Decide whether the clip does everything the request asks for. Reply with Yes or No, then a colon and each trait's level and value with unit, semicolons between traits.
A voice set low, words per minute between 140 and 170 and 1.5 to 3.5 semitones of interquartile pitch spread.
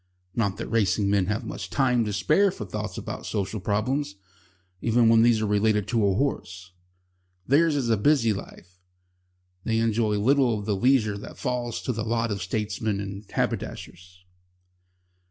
Yes: low, 110 Hz; average, 165 wpm; average, 3.0 semitones